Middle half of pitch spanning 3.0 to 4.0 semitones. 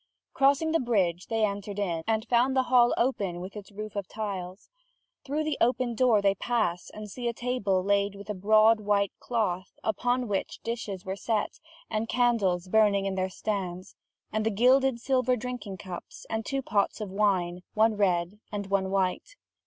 Yes: average, 3.6 semitones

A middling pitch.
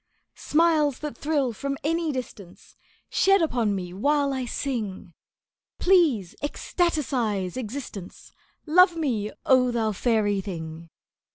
No: very high, 255 Hz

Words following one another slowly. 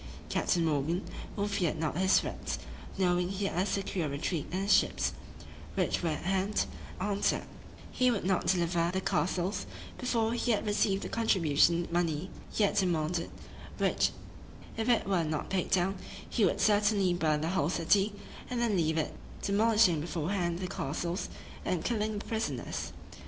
No: average, 160 wpm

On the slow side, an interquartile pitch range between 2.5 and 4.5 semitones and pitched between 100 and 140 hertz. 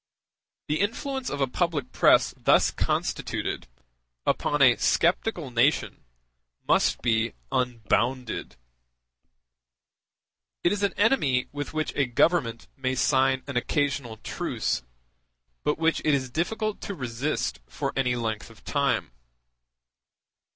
No: slow, 115 wpm; average, 4.9 semitones; low, 135 Hz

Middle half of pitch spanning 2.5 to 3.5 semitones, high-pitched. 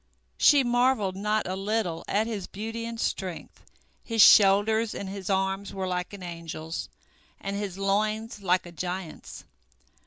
Yes: average, 2.8 semitones; high, 200 Hz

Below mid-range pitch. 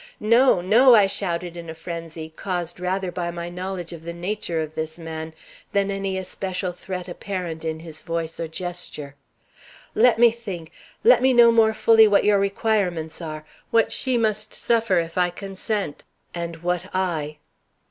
No: medium, 180 Hz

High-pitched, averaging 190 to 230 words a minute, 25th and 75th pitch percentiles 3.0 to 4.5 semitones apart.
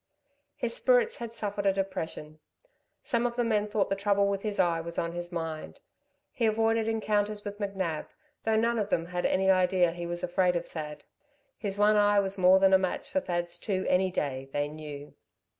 Yes: high, 195 Hz; average, 200 wpm; average, 3.4 semitones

